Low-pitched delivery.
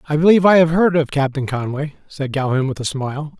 No: medium, 145 Hz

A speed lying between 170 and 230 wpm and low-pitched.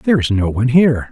No: fast, 270 wpm; low, 125 Hz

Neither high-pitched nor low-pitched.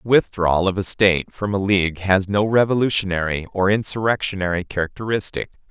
No: low, 100 Hz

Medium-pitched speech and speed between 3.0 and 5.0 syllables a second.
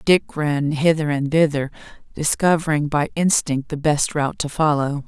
Yes: medium, 150 Hz; 4.7 syllables/s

